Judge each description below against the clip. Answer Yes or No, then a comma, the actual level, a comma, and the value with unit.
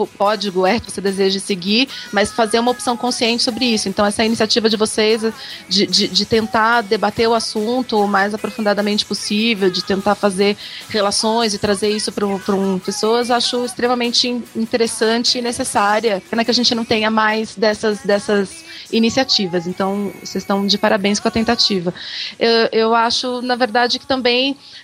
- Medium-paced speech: Yes, average, 170 wpm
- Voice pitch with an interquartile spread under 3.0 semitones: Yes, narrow, 2.6 semitones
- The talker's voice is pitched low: No, high, 220 Hz